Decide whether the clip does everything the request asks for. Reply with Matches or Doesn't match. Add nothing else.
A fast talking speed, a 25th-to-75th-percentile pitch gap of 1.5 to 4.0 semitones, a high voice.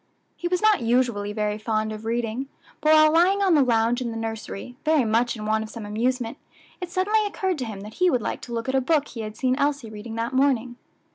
Doesn't match